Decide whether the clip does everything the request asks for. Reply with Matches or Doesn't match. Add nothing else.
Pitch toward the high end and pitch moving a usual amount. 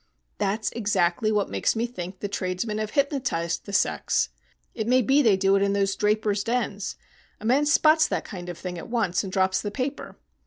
Matches